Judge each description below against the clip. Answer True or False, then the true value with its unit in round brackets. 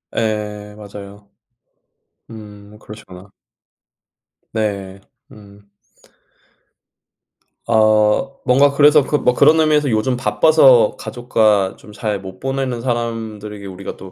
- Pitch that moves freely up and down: False (3.6 semitones)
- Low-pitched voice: True (110 Hz)